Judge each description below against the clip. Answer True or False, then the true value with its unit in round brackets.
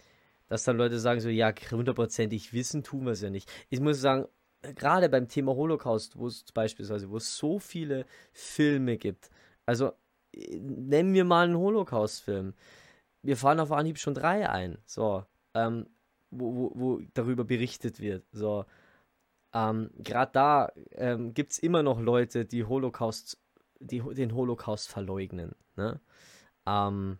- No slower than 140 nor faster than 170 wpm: True (145 wpm)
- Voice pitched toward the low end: True (120 Hz)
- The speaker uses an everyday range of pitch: True (4.1 semitones)